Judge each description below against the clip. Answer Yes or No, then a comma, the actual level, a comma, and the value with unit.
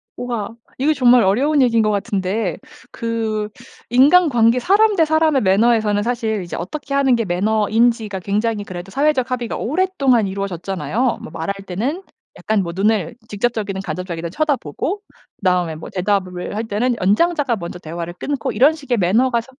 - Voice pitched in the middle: No, high, 225 Hz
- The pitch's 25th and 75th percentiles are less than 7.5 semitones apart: Yes, average, 5.1 semitones